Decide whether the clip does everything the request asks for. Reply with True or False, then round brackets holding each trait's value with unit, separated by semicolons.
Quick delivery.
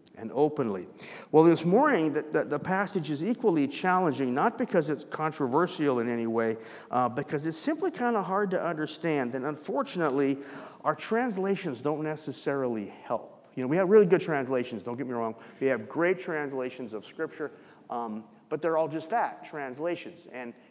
False (170 wpm)